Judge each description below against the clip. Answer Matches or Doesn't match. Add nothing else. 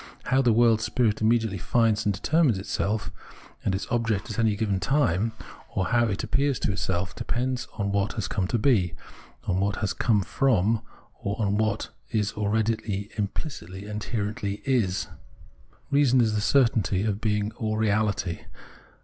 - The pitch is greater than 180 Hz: Doesn't match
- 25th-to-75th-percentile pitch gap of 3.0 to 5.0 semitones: Doesn't match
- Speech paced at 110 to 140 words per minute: Doesn't match